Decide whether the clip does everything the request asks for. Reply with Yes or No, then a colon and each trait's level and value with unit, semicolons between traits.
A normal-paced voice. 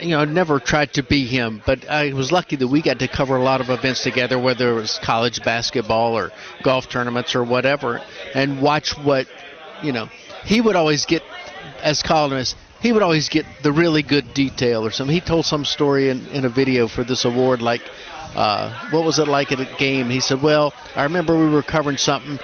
No: fast, 220 wpm